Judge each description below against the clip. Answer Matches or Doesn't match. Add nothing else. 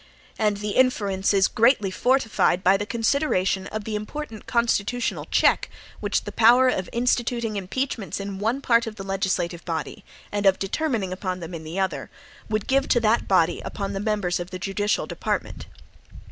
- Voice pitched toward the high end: Matches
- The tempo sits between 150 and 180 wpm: Matches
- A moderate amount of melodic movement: Matches